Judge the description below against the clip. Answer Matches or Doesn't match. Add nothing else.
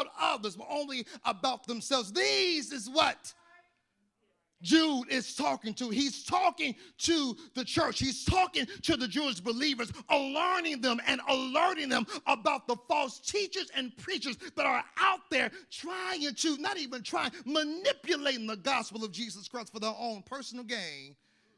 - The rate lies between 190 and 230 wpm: Doesn't match